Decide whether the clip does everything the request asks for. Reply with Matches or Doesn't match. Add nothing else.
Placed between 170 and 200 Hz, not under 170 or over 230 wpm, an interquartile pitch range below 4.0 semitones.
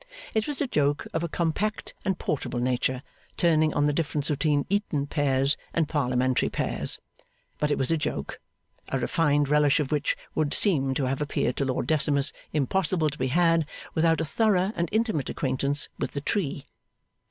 Doesn't match